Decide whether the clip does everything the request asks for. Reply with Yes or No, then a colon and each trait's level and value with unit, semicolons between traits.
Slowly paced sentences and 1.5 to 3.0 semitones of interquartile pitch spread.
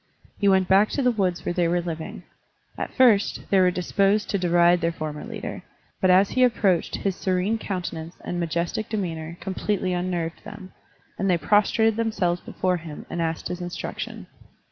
No: average, 175 wpm; average, 2.7 semitones